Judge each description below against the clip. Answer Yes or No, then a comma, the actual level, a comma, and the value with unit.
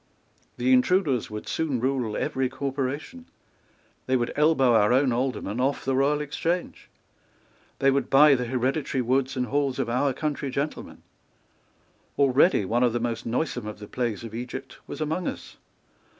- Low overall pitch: Yes, low, 130 Hz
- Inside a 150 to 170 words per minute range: Yes, average, 160 wpm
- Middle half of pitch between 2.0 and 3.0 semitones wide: Yes, average, 2.7 semitones